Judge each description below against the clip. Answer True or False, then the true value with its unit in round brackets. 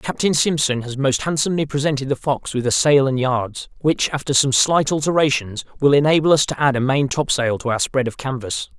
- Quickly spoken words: True (210 wpm)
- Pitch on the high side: False (135 Hz)